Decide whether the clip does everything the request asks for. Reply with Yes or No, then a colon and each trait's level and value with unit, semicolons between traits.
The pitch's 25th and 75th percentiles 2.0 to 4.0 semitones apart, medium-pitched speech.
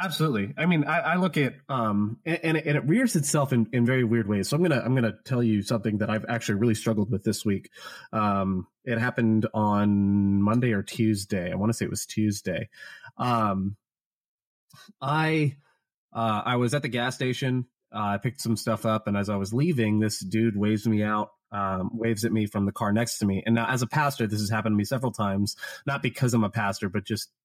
No: average, 3.5 semitones; low, 115 Hz